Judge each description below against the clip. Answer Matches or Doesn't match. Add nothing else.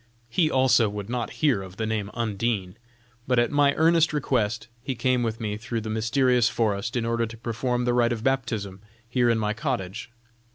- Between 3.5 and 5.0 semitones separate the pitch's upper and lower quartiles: Doesn't match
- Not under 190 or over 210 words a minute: Matches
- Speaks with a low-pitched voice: Matches